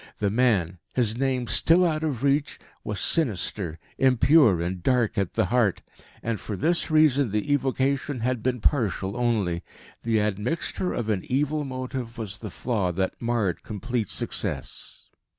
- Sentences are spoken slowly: No, average, 150 wpm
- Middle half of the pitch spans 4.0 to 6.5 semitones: Yes, average, 4.5 semitones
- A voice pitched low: Yes, low, 120 Hz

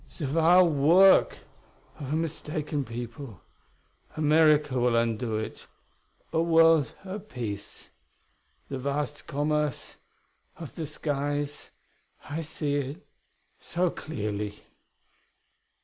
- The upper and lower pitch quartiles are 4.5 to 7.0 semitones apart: No, average, 3.9 semitones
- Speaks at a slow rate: Yes, slow, 100 wpm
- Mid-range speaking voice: Yes, medium, 145 Hz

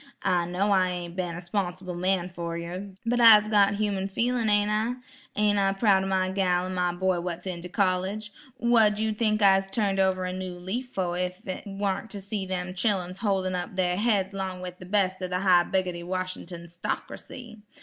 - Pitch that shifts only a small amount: Yes, narrow, 2.2 semitones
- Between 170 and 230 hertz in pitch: Yes, high, 190 Hz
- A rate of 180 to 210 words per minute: Yes, fast, 205 wpm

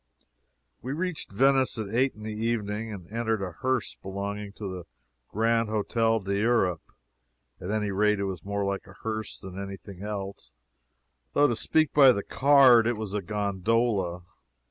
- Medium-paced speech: Yes, average, 165 wpm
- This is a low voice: Yes, low, 105 Hz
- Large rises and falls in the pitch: No, average, 2.8 semitones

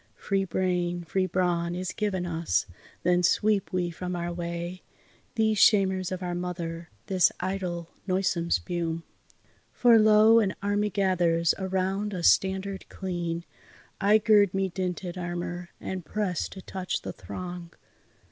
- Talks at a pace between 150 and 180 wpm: No, average, 140 wpm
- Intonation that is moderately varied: No, narrow, 1.9 semitones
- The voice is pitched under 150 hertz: No, medium, 185 Hz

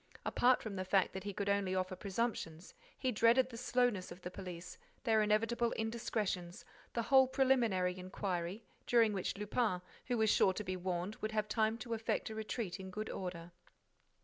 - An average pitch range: Yes, average, 3.8 semitones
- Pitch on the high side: Yes, high, 210 Hz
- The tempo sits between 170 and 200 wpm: Yes, average, 180 wpm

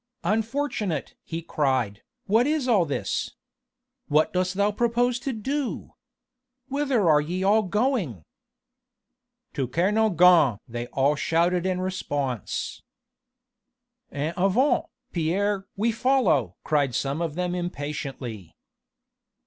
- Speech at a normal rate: No, slow, 110 wpm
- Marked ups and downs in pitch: Yes, wide, 7.0 semitones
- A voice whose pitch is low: No, medium, 180 Hz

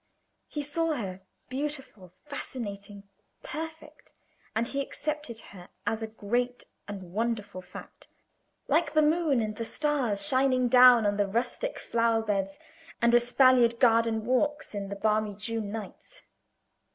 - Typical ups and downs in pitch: Yes, average, 4.7 semitones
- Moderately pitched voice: No, high, 235 Hz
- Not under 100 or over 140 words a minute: Yes, slow, 135 wpm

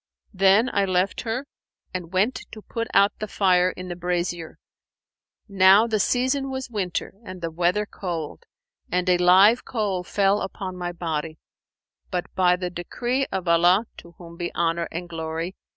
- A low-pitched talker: No, medium, 185 Hz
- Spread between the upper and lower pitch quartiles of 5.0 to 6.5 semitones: No, average, 3.0 semitones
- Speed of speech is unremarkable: Yes, average, 165 wpm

